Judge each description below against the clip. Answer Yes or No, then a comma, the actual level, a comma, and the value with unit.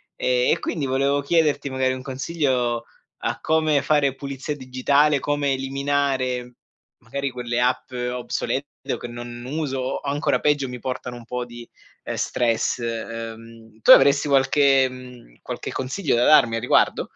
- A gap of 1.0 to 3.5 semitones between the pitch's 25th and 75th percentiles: Yes, narrow, 2.5 semitones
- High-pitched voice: No, low, 130 Hz